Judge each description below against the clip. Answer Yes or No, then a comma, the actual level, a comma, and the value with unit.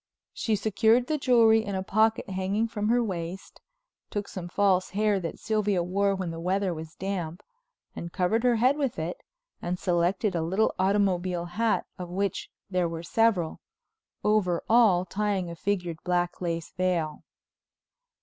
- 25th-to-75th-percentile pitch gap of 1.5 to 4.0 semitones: Yes, average, 3.4 semitones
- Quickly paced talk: No, average, 160 wpm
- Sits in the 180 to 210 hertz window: Yes, high, 190 Hz